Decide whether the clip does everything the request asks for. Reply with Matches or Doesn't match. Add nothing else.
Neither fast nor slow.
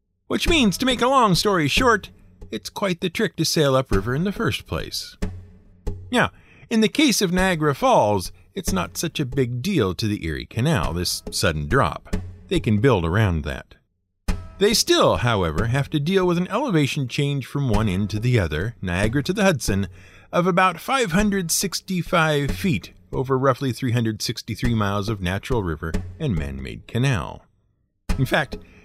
Matches